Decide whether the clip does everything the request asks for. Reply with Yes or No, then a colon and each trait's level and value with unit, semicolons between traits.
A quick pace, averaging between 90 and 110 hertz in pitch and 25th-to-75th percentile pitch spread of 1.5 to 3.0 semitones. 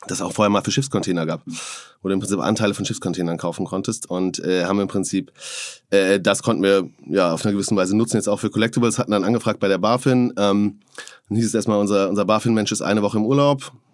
Yes: fast, 240 wpm; low, 105 Hz; narrow, 2.4 semitones